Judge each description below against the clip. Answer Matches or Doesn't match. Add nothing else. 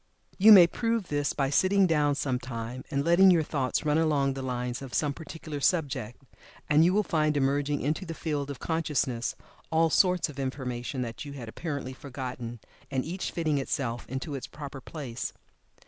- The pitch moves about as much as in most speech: Matches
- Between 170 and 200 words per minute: Matches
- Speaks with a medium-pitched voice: Matches